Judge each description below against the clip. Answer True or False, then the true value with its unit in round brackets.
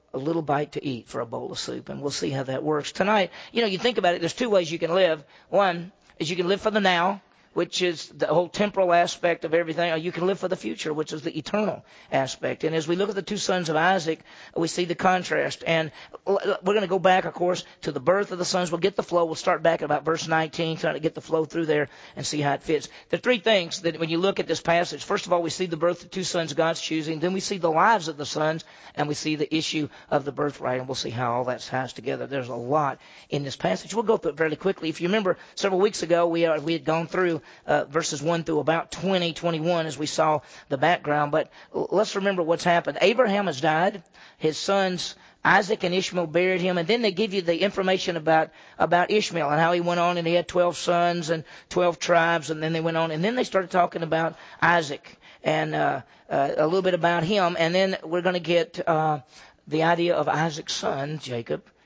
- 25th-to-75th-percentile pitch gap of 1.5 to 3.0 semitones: True (2.7 semitones)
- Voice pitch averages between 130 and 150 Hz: False (170 Hz)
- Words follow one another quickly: True (255 wpm)